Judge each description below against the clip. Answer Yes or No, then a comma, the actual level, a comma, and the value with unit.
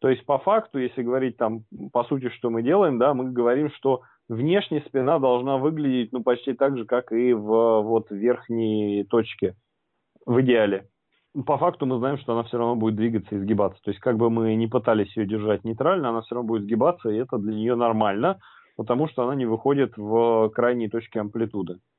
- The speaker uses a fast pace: Yes, fast, 200 wpm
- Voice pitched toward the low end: Yes, low, 120 Hz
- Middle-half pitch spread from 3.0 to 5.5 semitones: No, narrow, 2.6 semitones